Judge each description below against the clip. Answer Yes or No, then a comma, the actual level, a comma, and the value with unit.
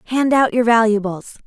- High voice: Yes, high, 230 Hz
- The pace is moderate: Yes, average, 165 wpm